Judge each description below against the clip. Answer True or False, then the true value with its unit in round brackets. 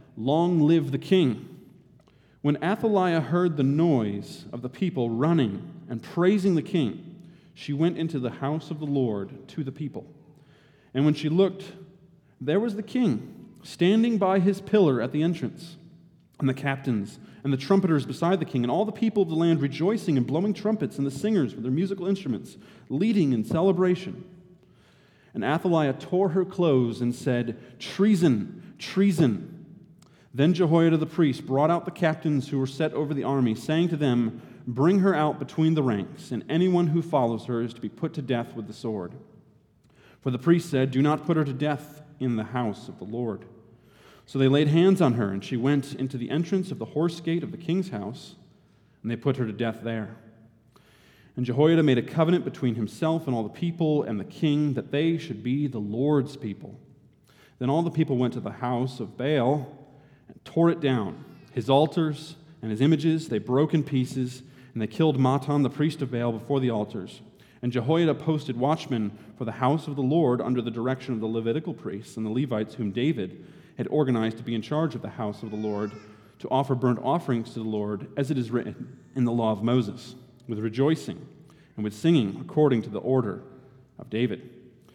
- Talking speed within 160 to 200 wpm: True (195 wpm)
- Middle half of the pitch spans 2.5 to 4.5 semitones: False (5.3 semitones)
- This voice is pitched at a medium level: True (145 Hz)